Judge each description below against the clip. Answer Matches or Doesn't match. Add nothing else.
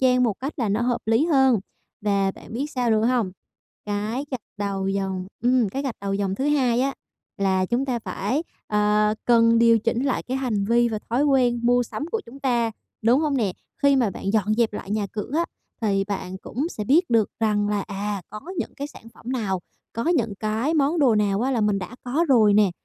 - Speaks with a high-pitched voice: Matches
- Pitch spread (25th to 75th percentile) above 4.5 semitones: Doesn't match